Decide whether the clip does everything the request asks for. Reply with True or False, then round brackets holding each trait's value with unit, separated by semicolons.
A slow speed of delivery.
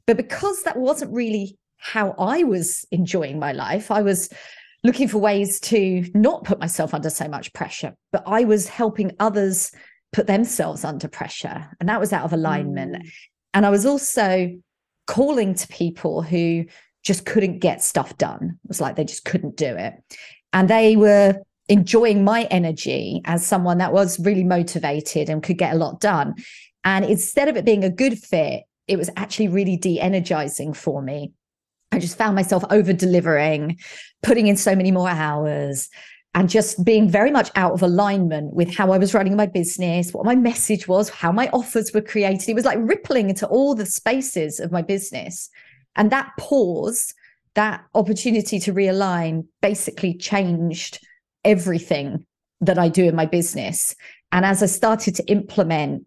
False (175 wpm)